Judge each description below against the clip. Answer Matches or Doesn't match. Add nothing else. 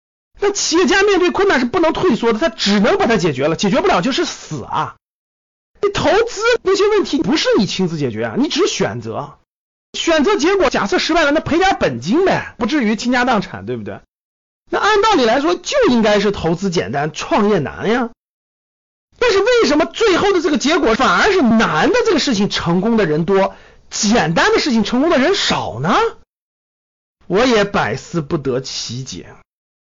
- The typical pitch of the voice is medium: Doesn't match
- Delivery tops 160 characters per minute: Matches